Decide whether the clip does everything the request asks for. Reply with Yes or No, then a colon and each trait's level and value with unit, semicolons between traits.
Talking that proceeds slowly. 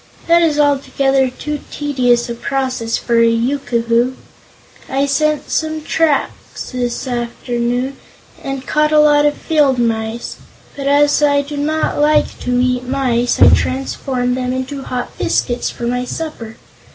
No: average, 145 wpm